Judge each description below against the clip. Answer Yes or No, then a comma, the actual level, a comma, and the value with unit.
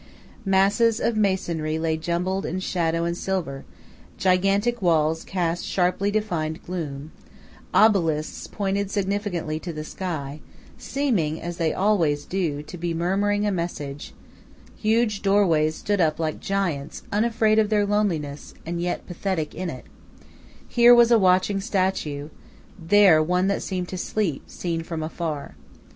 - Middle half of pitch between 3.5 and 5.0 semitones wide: Yes, average, 4.0 semitones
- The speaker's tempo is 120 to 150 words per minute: Yes, average, 140 wpm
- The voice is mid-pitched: Yes, medium, 180 Hz